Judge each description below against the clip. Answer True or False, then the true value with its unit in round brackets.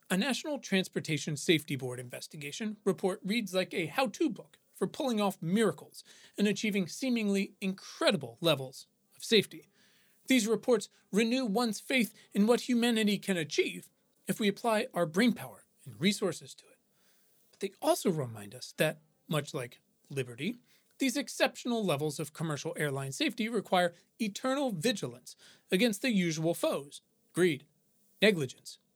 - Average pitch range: False (5.8 semitones)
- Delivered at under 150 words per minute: True (140 wpm)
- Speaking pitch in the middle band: False (200 Hz)